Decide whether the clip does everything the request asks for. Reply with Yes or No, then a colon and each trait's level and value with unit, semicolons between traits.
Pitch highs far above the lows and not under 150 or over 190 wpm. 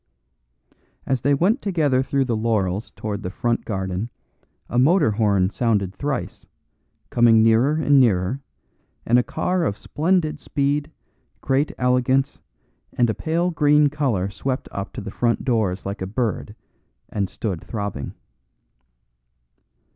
No: wide, 5.8 semitones; slow, 135 wpm